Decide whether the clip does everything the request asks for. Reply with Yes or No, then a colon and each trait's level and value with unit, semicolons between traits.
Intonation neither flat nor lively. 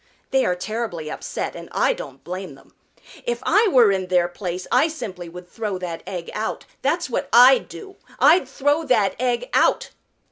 No: wide, 7.1 semitones